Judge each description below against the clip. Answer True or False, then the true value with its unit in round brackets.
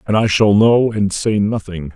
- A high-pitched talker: False (105 Hz)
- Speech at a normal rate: False (215 wpm)